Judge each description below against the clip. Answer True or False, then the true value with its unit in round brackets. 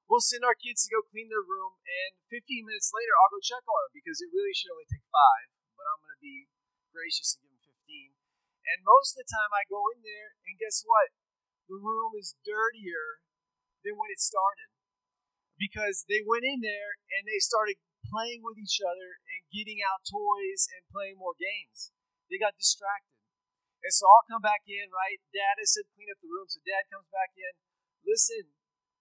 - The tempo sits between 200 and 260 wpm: True (205 wpm)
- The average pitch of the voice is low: False (215 Hz)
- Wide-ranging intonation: True (7.9 semitones)